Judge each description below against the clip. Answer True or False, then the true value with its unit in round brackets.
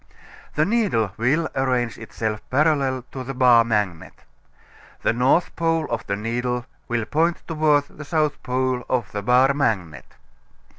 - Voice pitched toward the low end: True (130 Hz)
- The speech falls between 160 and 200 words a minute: False (145 wpm)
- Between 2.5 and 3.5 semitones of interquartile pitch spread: False (4.5 semitones)